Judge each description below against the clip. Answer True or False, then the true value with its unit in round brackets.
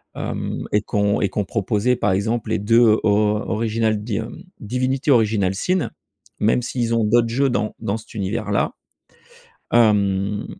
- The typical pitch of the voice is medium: False (110 Hz)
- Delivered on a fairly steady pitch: True (2.3 semitones)